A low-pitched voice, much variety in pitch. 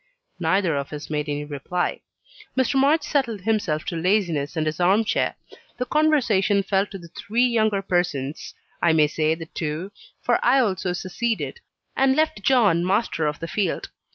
No: high, 190 Hz; wide, 6.1 semitones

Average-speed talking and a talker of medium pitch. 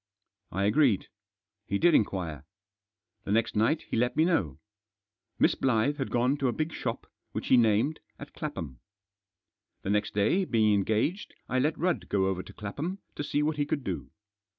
No: average, 180 wpm; low, 120 Hz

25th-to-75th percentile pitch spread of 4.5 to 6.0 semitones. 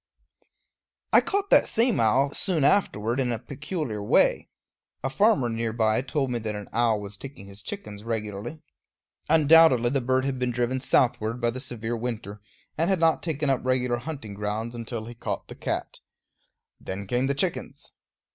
No: average, 4.0 semitones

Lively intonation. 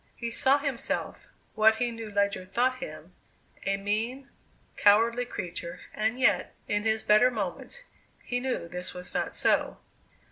No: average, 3.5 semitones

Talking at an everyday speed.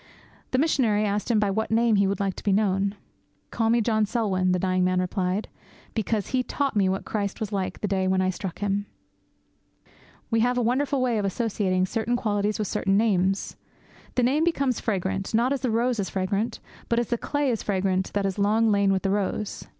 No: fast, 210 wpm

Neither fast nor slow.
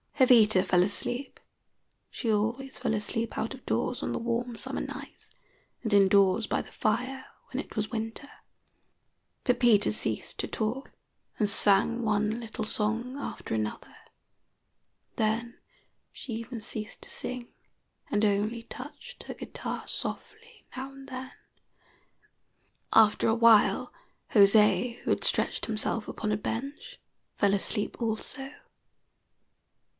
No: slow, 130 wpm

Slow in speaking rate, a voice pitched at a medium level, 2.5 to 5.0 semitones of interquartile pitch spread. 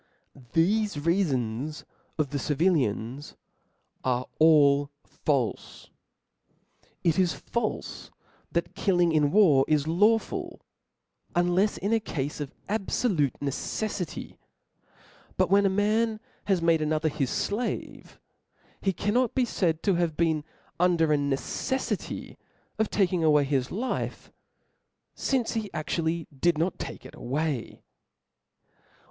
No: slow, 115 wpm; medium, 165 Hz; wide, 5.4 semitones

